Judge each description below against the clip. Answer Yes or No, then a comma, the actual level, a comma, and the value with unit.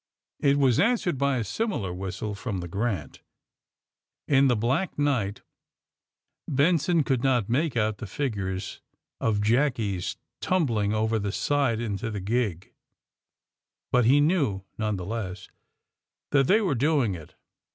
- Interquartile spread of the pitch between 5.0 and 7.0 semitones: Yes, wide, 5.6 semitones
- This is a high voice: No, low, 115 Hz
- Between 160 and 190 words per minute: No, average, 145 wpm